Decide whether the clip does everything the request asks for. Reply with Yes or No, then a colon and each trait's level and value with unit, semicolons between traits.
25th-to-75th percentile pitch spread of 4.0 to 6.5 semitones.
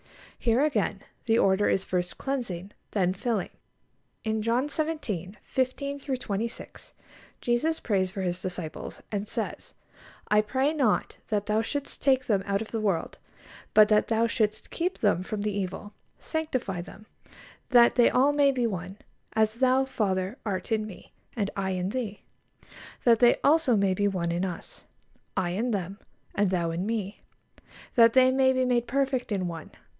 Yes: average, 4.9 semitones